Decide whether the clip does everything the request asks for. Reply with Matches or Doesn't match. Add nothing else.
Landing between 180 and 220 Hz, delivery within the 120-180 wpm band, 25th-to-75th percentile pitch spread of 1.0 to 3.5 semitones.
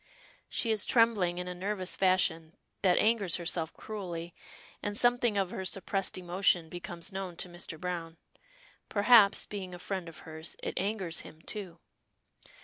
Matches